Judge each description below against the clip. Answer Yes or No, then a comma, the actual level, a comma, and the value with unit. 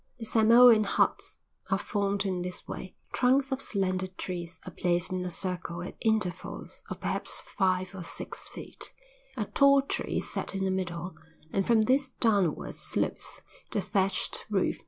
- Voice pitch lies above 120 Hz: Yes, high, 190 Hz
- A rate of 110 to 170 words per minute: Yes, average, 165 wpm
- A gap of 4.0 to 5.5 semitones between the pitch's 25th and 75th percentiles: No, average, 3.4 semitones